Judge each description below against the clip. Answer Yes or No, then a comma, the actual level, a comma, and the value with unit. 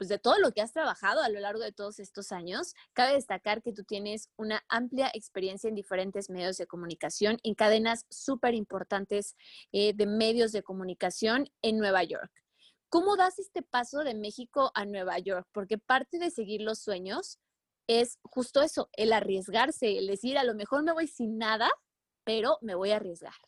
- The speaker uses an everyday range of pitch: Yes, average, 3.9 semitones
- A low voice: No, high, 220 Hz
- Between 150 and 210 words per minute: Yes, average, 185 wpm